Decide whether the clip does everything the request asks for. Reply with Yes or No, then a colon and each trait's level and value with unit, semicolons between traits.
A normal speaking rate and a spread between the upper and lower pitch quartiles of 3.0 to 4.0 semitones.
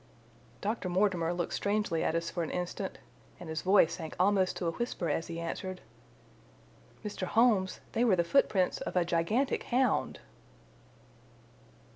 Yes: average, 150 wpm; average, 3.5 semitones